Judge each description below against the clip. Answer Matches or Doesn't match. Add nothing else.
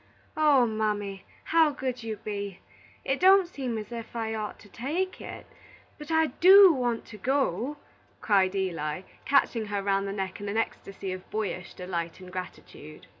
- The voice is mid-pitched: Doesn't match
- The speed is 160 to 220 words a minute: Matches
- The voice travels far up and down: Matches